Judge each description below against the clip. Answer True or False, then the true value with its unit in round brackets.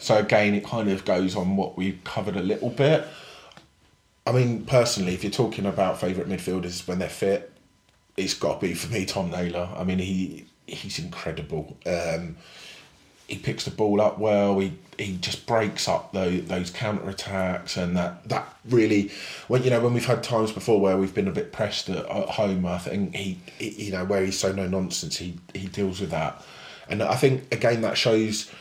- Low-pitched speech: True (95 Hz)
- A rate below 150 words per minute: False (200 wpm)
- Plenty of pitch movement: False (2.8 semitones)